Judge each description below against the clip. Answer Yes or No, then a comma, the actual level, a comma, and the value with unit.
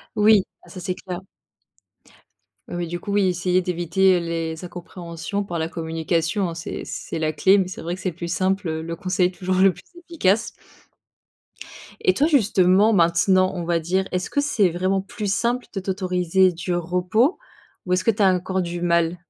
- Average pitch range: No, narrow, 2.2 semitones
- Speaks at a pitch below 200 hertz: Yes, medium, 185 Hz